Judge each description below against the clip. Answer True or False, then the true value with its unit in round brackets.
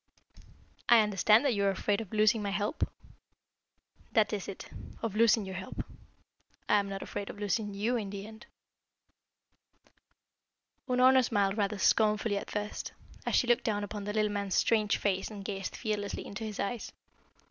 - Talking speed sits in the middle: True (170 wpm)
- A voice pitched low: False (210 Hz)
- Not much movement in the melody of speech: True (1.6 semitones)